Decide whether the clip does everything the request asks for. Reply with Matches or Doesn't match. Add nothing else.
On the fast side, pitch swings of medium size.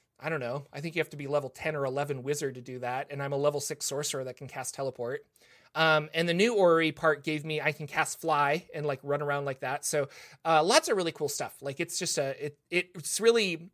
Doesn't match